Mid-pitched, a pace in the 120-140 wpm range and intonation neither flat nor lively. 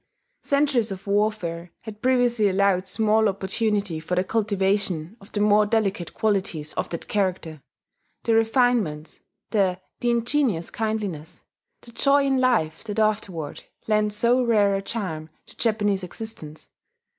No: high, 205 Hz; slow, 135 wpm; average, 3.6 semitones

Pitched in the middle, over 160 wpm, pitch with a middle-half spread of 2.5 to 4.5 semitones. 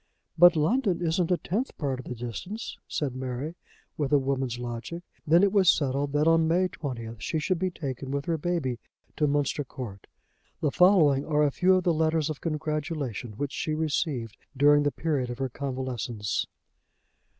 Yes: medium, 145 Hz; average, 180 wpm; average, 4.1 semitones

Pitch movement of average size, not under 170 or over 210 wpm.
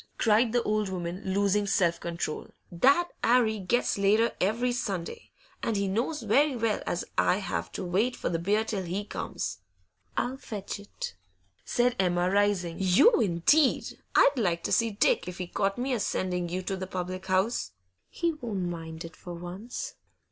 Yes: average, 4.4 semitones; average, 175 wpm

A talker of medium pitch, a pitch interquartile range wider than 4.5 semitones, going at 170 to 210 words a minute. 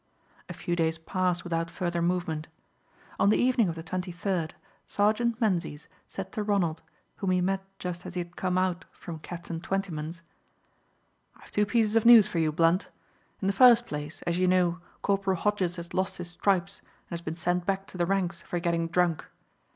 No: medium, 180 Hz; narrow, 2.5 semitones; average, 190 wpm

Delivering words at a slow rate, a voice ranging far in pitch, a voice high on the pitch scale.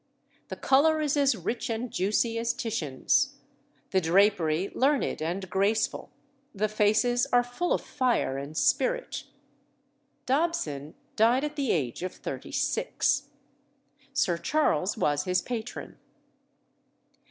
Yes: slow, 120 wpm; wide, 6.4 semitones; high, 220 Hz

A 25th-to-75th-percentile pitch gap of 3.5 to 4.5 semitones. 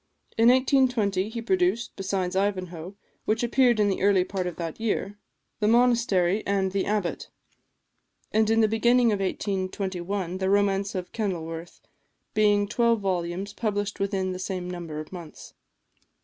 No: average, 3.0 semitones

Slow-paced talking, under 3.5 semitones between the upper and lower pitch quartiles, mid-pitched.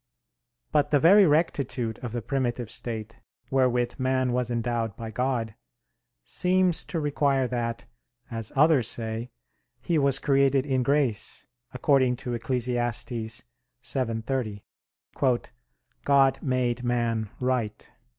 No: slow, 110 wpm; average, 2.8 semitones; low, 125 Hz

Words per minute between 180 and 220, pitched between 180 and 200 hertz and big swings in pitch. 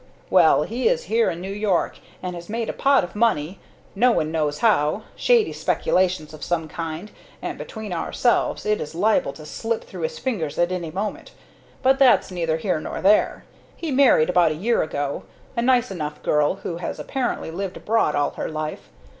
Yes: average, 190 wpm; medium, 185 Hz; wide, 6.4 semitones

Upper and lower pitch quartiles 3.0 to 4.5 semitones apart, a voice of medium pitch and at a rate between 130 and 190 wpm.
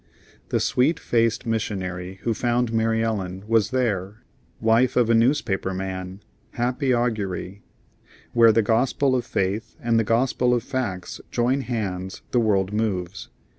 No: average, 4.0 semitones; low, 115 Hz; average, 140 wpm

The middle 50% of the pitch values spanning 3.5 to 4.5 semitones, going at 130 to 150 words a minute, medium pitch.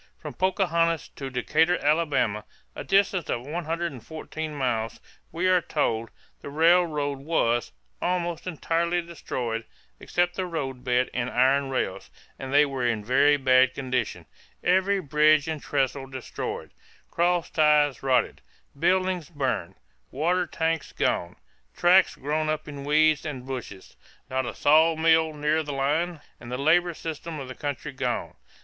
Yes: average, 4.1 semitones; average, 145 wpm; medium, 150 Hz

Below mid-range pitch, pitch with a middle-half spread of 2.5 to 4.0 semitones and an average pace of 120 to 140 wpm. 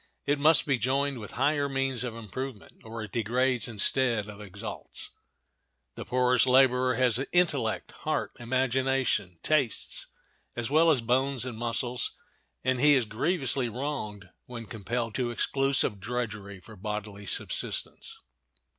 Yes: low, 125 Hz; average, 3.4 semitones; slow, 135 wpm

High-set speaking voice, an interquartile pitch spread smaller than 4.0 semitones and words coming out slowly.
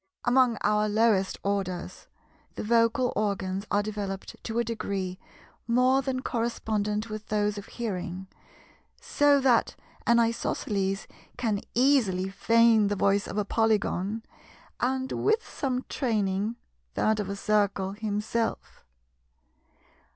Yes: high, 215 Hz; average, 2.8 semitones; slow, 120 wpm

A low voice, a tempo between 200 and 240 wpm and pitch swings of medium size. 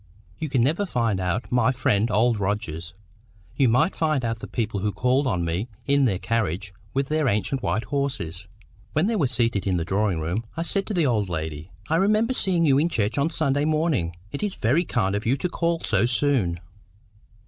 No: low, 120 Hz; fast, 205 wpm; wide, 6.9 semitones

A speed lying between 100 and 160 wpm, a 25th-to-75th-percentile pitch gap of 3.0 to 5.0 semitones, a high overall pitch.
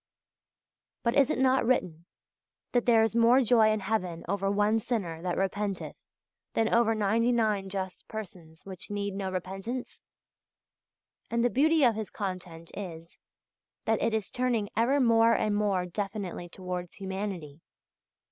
Yes: average, 145 wpm; average, 3.6 semitones; high, 205 Hz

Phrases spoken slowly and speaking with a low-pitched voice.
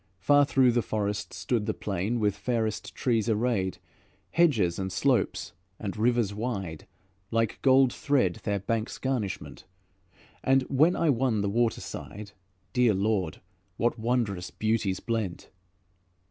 Yes: slow, 130 wpm; low, 110 Hz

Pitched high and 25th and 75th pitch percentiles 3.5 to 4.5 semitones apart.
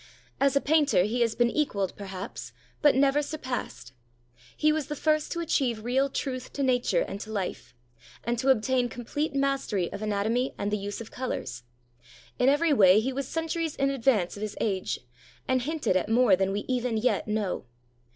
No: very high, 250 Hz; average, 5.0 semitones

